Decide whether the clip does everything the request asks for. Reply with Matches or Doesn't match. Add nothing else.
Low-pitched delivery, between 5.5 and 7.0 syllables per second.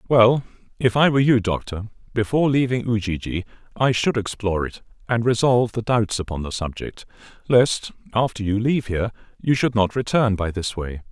Matches